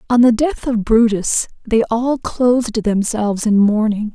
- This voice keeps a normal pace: Yes, average, 160 wpm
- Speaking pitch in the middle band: No, high, 225 Hz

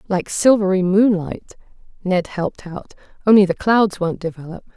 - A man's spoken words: No, female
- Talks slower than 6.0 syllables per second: Yes, 5.0 syllables/s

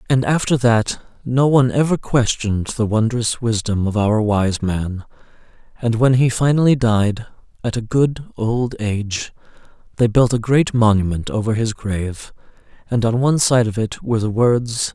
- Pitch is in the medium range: No, low, 115 Hz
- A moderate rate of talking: Yes, average, 165 wpm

